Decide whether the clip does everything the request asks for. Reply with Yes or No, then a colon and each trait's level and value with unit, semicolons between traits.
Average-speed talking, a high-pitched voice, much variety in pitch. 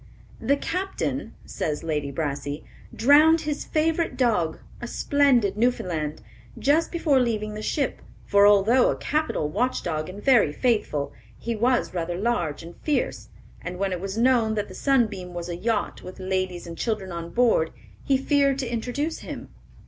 Yes: average, 160 wpm; high, 220 Hz; wide, 7.1 semitones